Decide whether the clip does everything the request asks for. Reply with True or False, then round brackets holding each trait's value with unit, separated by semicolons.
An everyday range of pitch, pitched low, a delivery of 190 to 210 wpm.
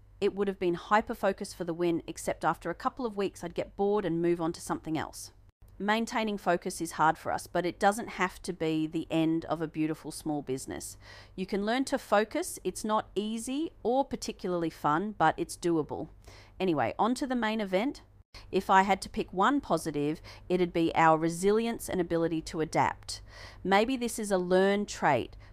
False (4.7 semitones; 180 Hz; 195 wpm)